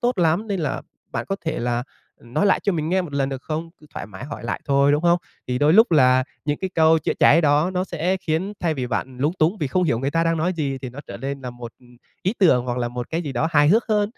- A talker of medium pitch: Yes, medium, 155 Hz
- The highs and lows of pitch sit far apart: No, average, 4.7 semitones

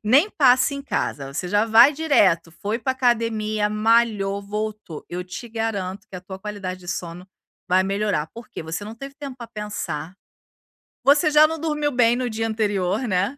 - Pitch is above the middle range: Yes, high, 215 Hz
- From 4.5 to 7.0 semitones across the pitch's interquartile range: Yes, average, 4.8 semitones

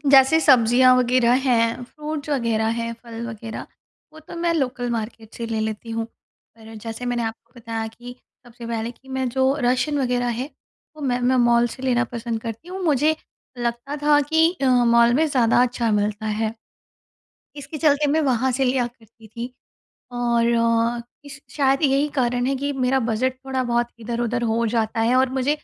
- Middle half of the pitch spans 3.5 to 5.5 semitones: No, narrow, 2.6 semitones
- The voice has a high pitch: Yes, high, 245 Hz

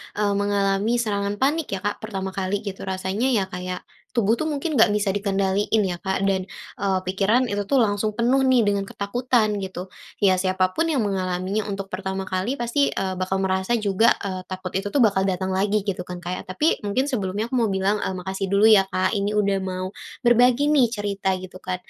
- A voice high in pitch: Yes, high, 200 Hz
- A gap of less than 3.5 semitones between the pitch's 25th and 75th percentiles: Yes, narrow, 2.6 semitones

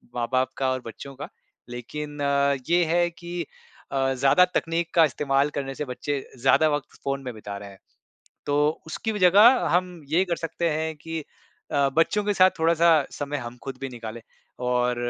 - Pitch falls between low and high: Yes, medium, 145 Hz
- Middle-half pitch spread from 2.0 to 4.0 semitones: No, average, 4.4 semitones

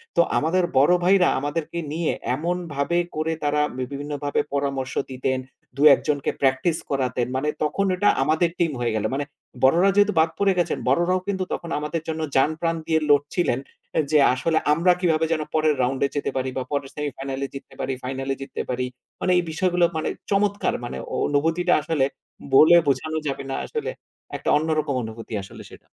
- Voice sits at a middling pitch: Yes, medium, 150 Hz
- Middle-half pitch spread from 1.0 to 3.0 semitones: No, average, 3.9 semitones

